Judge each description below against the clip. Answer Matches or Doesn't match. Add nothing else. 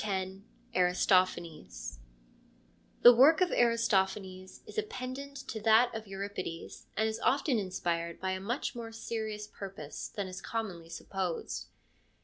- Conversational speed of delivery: Doesn't match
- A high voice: Matches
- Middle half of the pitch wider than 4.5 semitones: Doesn't match